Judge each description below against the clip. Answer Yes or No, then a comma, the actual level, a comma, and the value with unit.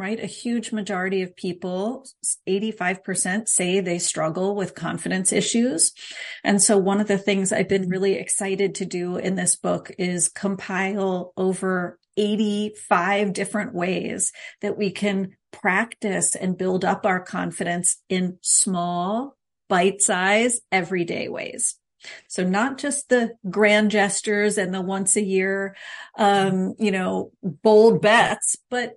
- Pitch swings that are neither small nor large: No, narrow, 2.2 semitones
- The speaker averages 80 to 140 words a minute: Yes, slow, 135 wpm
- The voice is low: No, high, 195 Hz